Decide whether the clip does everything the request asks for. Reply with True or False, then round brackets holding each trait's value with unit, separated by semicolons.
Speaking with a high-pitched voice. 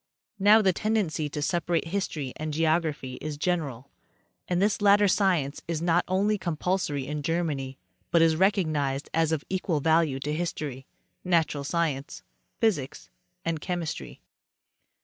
False (165 Hz)